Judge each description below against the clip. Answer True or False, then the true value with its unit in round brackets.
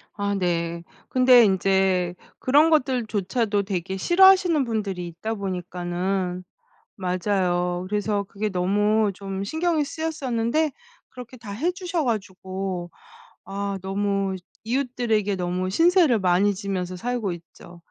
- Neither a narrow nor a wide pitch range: True (5.0 semitones)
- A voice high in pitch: True (200 Hz)